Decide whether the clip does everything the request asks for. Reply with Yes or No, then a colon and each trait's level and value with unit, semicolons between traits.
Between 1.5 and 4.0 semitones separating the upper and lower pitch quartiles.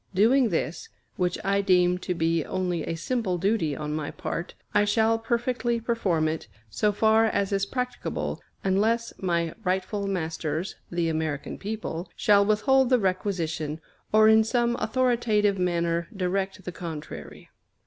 No: average, 4.6 semitones